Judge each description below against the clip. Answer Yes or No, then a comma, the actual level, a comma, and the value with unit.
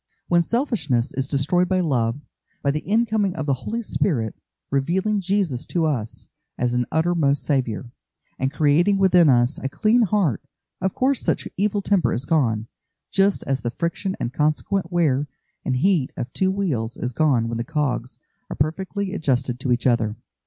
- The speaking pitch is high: No, medium, 150 Hz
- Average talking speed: Yes, average, 170 wpm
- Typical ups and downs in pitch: No, wide, 7.0 semitones